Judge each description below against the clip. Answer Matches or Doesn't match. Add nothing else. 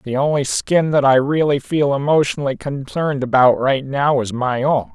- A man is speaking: Matches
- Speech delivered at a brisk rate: Doesn't match